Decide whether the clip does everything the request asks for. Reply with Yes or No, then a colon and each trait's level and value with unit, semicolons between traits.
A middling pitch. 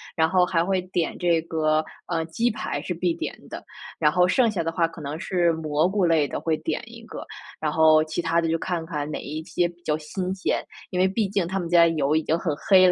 Yes: medium, 165 Hz